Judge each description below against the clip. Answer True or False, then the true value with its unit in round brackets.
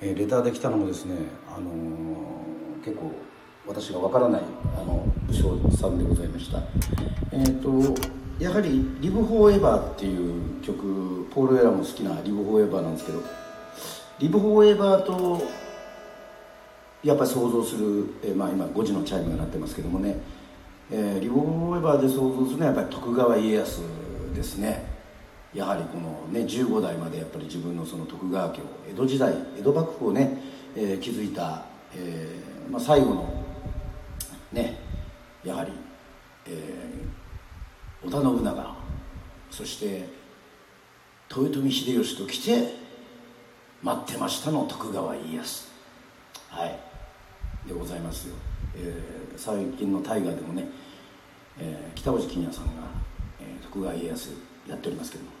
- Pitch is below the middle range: True (100 Hz)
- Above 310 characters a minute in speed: False (295 characters per minute)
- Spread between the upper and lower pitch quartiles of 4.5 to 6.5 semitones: False (7.4 semitones)